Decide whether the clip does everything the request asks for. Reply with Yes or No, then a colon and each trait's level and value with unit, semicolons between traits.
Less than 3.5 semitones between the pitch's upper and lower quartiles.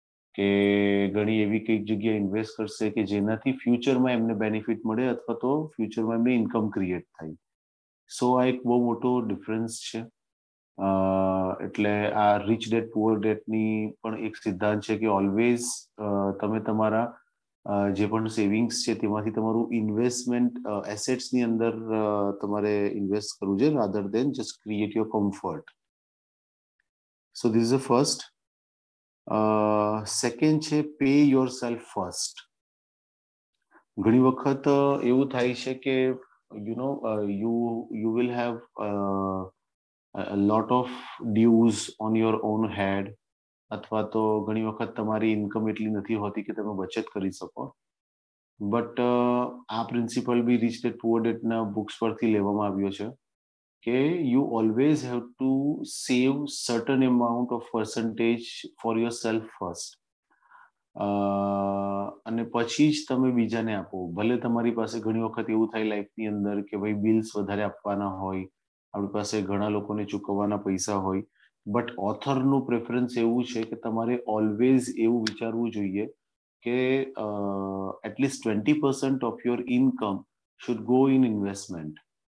Yes: average, 2.7 semitones